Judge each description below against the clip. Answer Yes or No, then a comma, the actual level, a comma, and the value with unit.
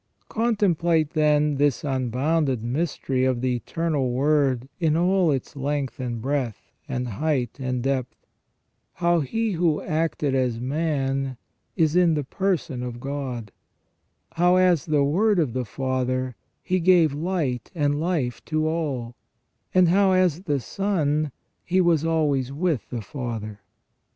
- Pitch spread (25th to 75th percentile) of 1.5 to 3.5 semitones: No, average, 4.5 semitones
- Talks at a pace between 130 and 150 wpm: Yes, average, 140 wpm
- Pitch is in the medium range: Yes, medium, 145 Hz